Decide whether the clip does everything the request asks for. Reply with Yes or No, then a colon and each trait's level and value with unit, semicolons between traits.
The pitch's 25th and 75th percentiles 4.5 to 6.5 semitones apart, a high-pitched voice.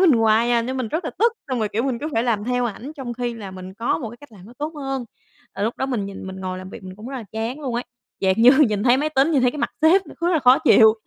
No: average, 3.9 semitones; high, 240 Hz